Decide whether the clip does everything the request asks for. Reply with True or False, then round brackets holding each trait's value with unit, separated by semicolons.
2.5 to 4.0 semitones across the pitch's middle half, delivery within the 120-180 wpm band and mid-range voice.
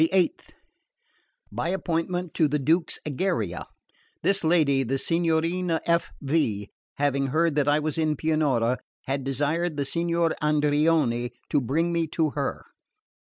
True (3.3 semitones; 135 wpm; 155 Hz)